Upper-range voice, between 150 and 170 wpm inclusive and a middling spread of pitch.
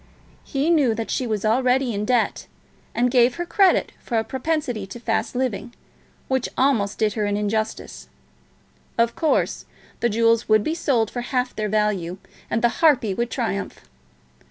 Yes: high, 235 Hz; average, 165 wpm; average, 3.2 semitones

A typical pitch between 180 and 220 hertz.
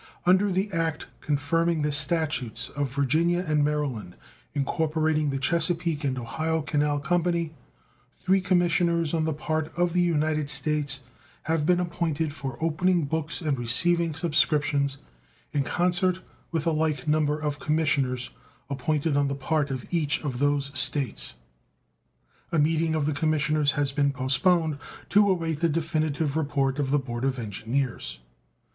No: medium, 155 Hz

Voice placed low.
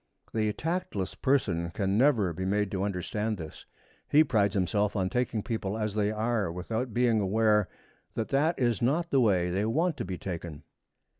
Yes: low, 105 Hz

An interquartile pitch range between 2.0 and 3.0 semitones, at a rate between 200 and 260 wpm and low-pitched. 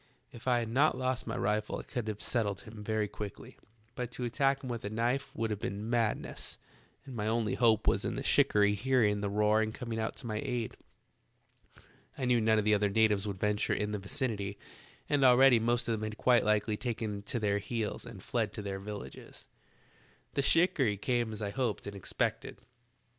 Yes: average, 2.7 semitones; fast, 205 wpm; low, 110 Hz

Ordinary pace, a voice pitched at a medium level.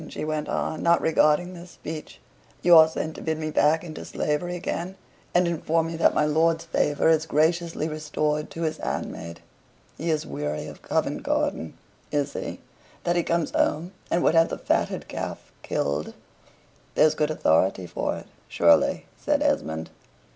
Yes: average, 170 wpm; medium, 155 Hz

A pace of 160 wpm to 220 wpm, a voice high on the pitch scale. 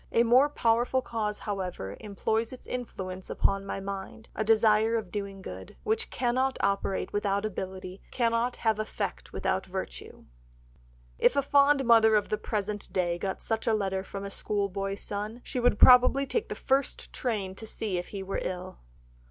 Yes: average, 170 wpm; high, 210 Hz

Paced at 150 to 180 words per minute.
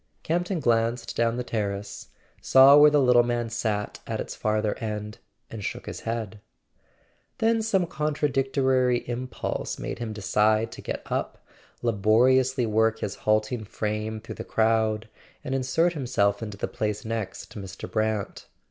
Yes: average, 155 wpm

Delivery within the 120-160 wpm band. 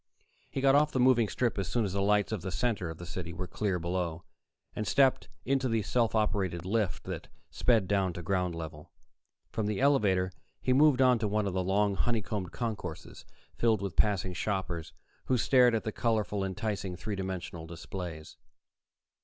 No: average, 185 wpm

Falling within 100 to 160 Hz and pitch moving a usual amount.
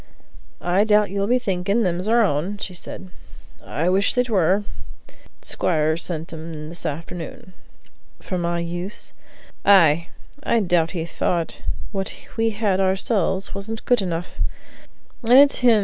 No: medium, 185 Hz; average, 3.2 semitones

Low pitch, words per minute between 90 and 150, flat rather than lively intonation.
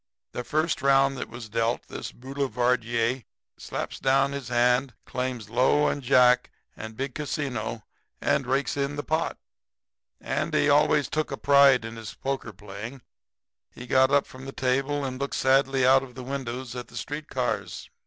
No: low, 130 Hz; average, 165 wpm; narrow, 2.2 semitones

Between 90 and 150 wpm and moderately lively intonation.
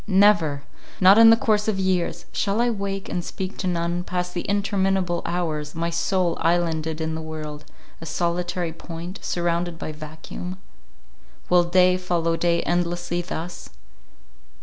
No: average, 140 wpm; narrow, 2.1 semitones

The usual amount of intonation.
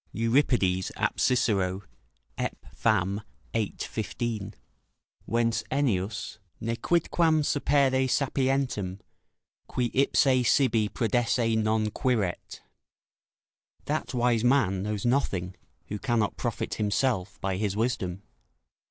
Yes: average, 4.4 semitones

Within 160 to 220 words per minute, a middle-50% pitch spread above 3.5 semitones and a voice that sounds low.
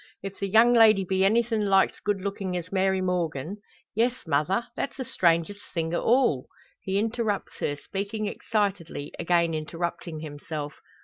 No: average, 165 wpm; average, 4.0 semitones; high, 190 Hz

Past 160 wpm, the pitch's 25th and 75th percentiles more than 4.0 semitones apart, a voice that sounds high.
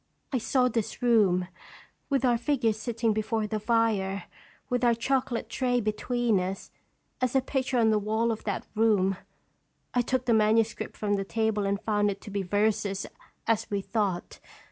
No: average, 170 wpm; average, 2.8 semitones; high, 220 Hz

